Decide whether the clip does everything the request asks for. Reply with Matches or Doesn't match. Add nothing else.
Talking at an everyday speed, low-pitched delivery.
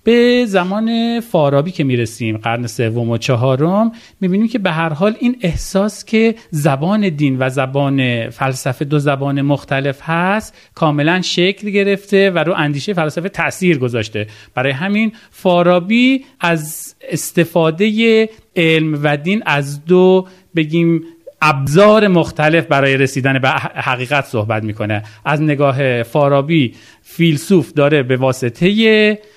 Doesn't match